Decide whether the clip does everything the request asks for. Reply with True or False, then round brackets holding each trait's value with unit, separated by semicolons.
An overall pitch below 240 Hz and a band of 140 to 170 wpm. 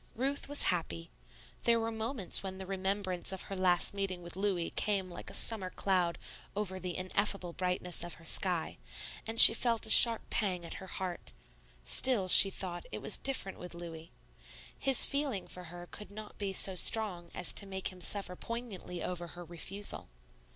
False (190 Hz; 180 wpm)